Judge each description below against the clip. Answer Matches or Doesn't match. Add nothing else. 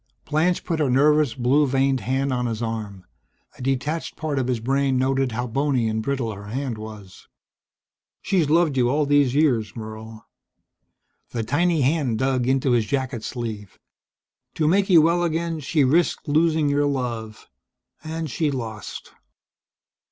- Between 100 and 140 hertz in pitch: Matches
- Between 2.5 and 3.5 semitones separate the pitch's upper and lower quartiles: Doesn't match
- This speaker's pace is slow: Doesn't match